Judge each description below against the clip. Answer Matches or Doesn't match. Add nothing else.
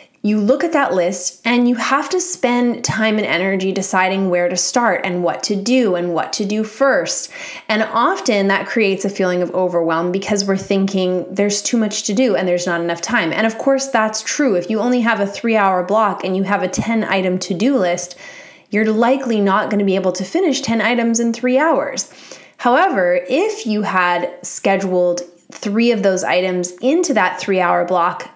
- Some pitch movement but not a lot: Matches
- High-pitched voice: Matches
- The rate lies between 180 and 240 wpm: Matches